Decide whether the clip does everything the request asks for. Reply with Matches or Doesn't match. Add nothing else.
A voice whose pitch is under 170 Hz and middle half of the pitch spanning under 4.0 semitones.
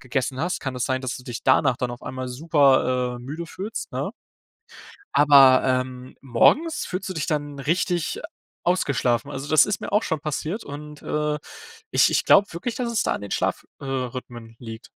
Doesn't match